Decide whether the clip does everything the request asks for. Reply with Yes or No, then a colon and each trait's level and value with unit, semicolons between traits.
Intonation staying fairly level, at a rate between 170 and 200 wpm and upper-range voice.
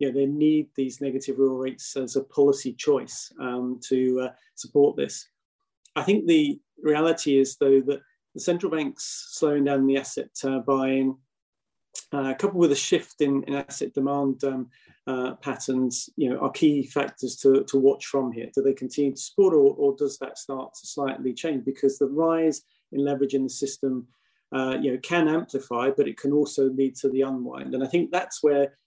No: narrow, 2.2 semitones; average, 195 wpm; low, 135 Hz